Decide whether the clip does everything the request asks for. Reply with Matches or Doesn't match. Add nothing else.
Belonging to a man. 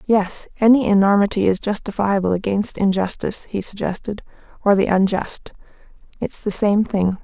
Doesn't match